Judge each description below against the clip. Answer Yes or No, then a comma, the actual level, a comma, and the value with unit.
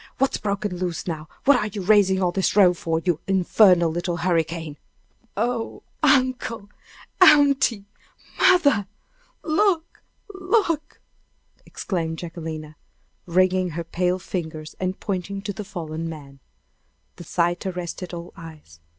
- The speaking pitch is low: No, medium, 185 Hz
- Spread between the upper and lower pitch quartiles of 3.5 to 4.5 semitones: Yes, average, 4.2 semitones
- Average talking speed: No, slow, 125 wpm